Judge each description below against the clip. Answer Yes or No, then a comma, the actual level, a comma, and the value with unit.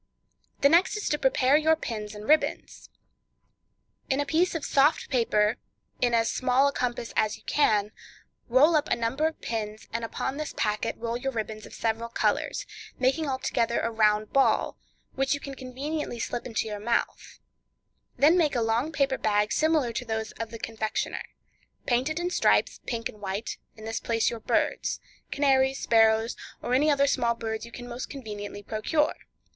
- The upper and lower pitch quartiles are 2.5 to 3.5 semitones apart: No, average, 4.1 semitones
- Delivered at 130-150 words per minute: No, average, 175 wpm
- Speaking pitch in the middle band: No, high, 240 Hz